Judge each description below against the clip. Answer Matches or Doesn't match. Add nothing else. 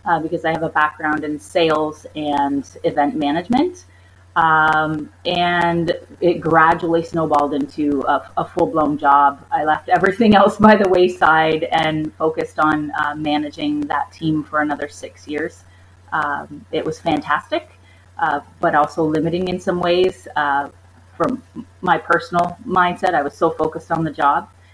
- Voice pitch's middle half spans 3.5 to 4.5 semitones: Doesn't match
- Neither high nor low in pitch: Matches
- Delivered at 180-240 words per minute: Doesn't match